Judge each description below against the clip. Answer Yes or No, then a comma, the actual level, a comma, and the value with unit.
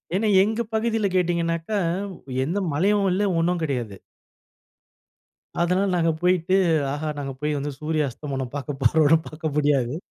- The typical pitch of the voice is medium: Yes, medium, 160 Hz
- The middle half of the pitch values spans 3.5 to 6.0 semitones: Yes, average, 4.0 semitones